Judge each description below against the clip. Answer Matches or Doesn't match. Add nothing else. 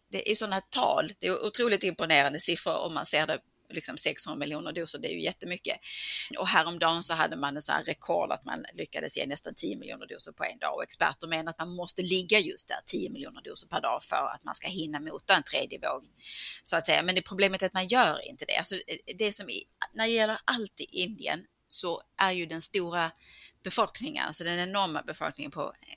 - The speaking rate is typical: Doesn't match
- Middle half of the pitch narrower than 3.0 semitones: Doesn't match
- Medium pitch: Matches